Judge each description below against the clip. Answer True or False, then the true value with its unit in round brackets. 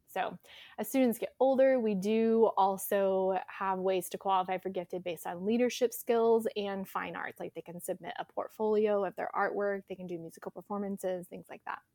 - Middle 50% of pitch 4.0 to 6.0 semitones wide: False (2.7 semitones)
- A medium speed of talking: True (190 wpm)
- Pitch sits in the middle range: False (195 Hz)